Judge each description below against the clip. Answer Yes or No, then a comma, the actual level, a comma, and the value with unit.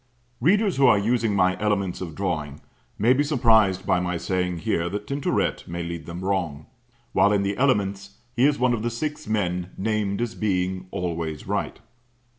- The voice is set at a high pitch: No, low, 100 Hz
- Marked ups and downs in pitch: No, average, 4.1 semitones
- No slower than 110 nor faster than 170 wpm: No, average, 180 wpm